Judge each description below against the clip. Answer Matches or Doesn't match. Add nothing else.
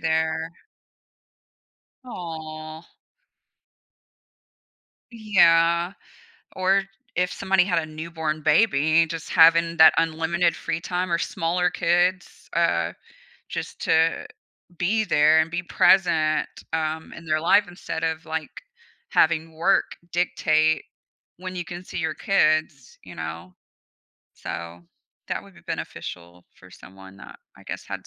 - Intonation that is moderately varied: Doesn't match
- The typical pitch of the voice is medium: Matches